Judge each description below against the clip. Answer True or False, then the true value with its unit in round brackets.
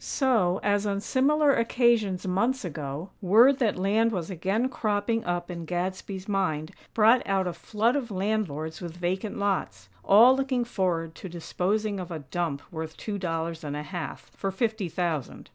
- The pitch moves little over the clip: False (4.3 semitones)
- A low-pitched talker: False (190 Hz)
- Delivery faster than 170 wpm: False (165 wpm)